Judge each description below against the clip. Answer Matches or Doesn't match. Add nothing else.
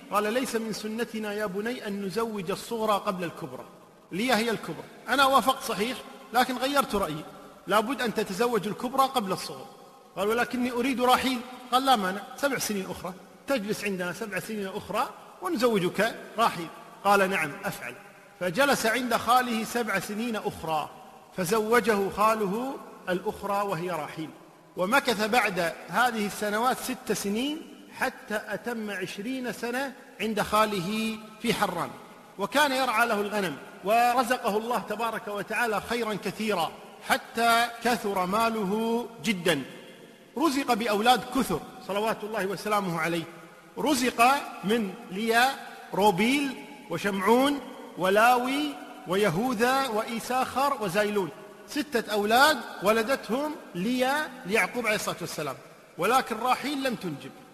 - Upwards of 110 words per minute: Matches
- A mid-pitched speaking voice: Doesn't match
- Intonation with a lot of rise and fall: Doesn't match